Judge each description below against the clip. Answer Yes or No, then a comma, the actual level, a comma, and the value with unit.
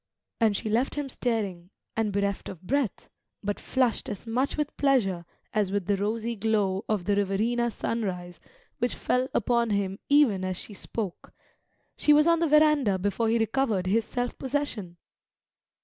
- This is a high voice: Yes, high, 220 Hz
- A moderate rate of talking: Yes, average, 165 wpm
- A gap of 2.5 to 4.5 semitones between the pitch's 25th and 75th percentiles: Yes, average, 4.1 semitones